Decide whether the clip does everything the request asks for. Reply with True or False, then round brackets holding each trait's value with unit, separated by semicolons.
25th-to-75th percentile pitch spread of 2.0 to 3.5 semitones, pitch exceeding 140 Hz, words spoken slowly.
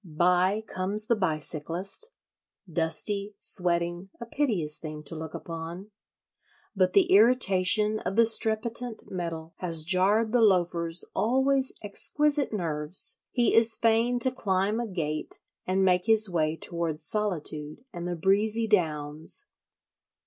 False (4.8 semitones; 185 Hz; 125 wpm)